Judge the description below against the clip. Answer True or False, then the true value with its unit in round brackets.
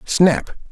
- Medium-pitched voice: True (170 Hz)